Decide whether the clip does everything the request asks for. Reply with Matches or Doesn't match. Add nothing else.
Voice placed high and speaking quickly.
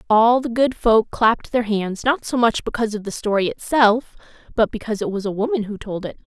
Matches